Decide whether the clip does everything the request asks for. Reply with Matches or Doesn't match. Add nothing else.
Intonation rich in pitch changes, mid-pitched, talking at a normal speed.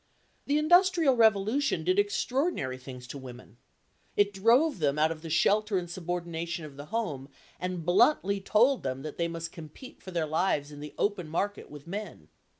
Matches